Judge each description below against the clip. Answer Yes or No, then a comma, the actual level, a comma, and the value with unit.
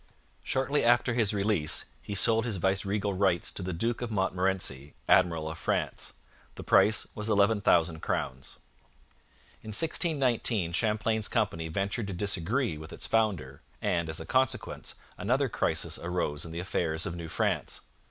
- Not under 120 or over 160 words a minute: Yes, average, 150 wpm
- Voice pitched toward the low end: Yes, low, 100 Hz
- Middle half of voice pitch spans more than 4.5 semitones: Yes, average, 5.1 semitones